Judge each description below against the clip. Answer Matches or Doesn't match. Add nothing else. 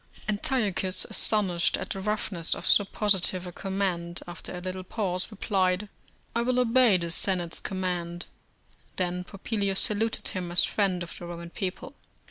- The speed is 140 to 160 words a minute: Matches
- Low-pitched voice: Doesn't match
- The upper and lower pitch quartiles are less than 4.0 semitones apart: Matches